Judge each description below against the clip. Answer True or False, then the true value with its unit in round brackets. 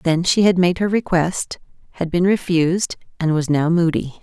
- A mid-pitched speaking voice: True (175 Hz)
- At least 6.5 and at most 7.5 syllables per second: False (4.9 syllables/s)